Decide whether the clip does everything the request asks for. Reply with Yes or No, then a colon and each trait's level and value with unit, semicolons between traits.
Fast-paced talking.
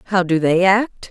Yes: fast, 215 wpm